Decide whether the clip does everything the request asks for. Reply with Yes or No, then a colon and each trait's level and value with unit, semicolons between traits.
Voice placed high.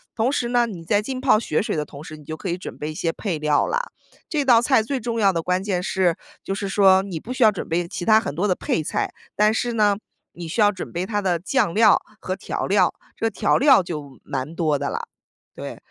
Yes: high, 195 Hz